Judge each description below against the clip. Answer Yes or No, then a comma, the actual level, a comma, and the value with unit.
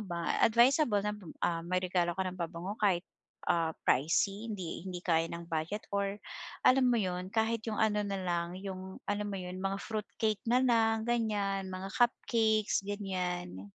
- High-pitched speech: Yes, high, 195 Hz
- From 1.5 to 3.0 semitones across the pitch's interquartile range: No, average, 3.4 semitones